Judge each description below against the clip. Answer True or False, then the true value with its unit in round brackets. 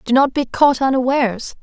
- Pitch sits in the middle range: False (260 Hz)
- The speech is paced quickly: False (185 wpm)